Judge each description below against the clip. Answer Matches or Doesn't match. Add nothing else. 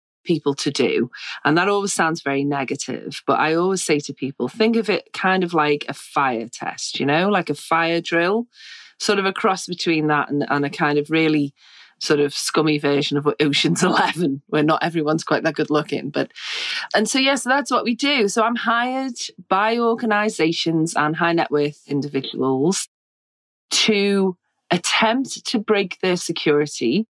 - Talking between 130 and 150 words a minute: Doesn't match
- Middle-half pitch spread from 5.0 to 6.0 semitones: Matches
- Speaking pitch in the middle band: Matches